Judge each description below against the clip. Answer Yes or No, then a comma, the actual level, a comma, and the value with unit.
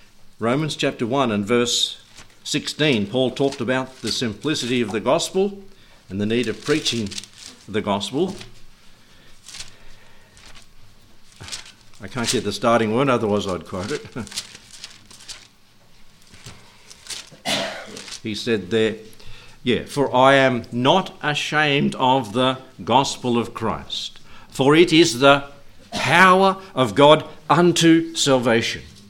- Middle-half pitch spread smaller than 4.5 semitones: No, average, 5.1 semitones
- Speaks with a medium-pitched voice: No, low, 115 Hz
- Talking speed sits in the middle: No, slow, 110 wpm